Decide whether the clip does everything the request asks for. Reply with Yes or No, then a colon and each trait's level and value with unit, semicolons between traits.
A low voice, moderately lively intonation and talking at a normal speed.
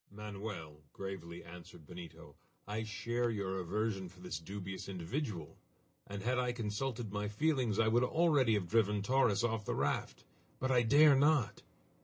Yes: low, 105 Hz; average, 4.3 semitones; average, 155 wpm